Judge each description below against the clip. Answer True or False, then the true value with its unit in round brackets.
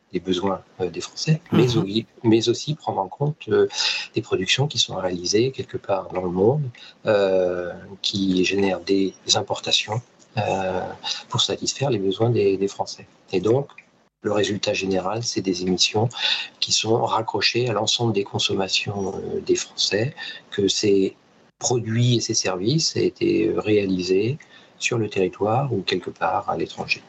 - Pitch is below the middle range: True (110 Hz)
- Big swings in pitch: True (7.2 semitones)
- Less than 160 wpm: True (145 wpm)